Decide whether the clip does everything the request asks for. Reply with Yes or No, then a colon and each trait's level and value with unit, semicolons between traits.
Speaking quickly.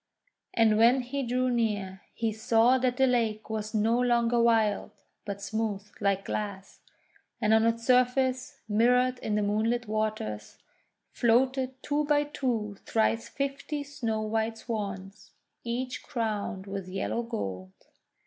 No: slow, 135 wpm